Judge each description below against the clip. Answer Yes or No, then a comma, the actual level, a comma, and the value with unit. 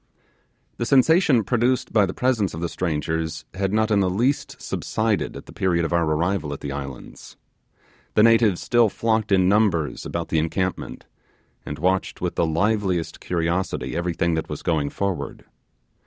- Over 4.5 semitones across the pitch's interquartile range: Yes, average, 5.1 semitones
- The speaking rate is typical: Yes, average, 165 wpm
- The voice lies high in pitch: No, very low, 95 Hz